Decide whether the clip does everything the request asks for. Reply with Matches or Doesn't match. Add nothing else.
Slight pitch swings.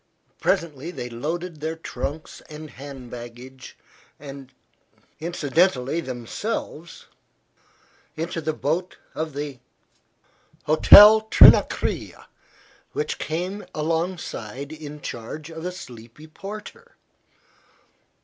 Doesn't match